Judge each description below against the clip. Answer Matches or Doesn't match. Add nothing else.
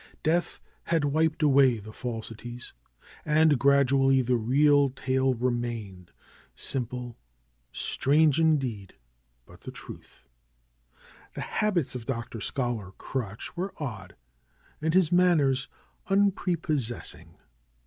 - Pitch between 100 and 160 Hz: Matches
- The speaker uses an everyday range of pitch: Matches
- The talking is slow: Matches